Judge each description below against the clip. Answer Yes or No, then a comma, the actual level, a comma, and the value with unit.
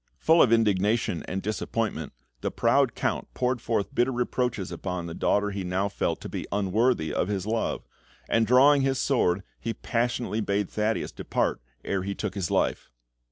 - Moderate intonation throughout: Yes, average, 3.9 semitones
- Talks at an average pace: Yes, average, 170 wpm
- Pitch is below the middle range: Yes, low, 105 Hz